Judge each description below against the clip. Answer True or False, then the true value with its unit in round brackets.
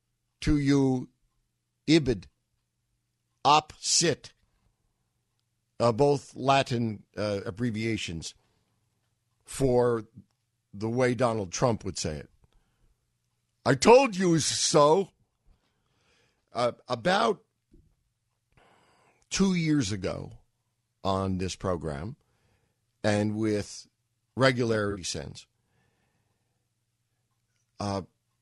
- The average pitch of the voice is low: True (115 Hz)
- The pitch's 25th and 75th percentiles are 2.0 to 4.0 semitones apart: True (2.8 semitones)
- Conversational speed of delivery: False (75 wpm)